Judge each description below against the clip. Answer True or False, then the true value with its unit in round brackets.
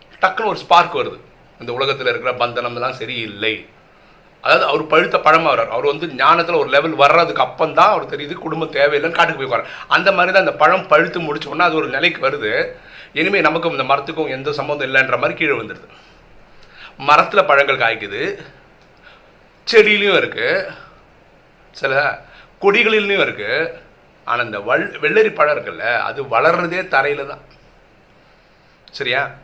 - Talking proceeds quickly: True (140 wpm)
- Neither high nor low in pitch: True (170 Hz)